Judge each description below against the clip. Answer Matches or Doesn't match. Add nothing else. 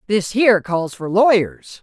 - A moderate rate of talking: Matches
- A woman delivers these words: Matches